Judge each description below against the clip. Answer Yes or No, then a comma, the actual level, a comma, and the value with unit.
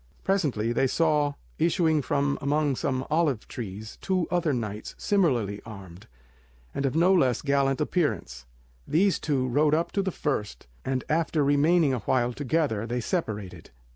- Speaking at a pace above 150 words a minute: No, average, 145 wpm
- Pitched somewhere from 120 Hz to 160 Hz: Yes, medium, 140 Hz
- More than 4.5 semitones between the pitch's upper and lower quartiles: Yes, average, 5.3 semitones